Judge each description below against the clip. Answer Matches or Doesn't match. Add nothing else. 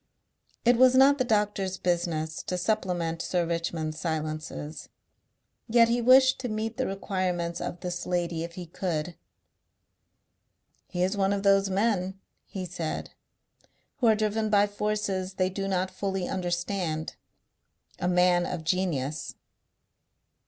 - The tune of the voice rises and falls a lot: Doesn't match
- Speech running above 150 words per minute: Doesn't match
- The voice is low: Doesn't match